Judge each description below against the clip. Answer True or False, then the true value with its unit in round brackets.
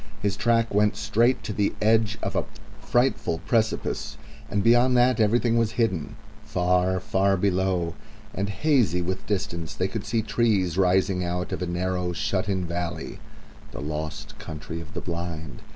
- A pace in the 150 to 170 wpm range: True (160 wpm)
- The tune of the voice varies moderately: True (3.9 semitones)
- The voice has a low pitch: True (95 Hz)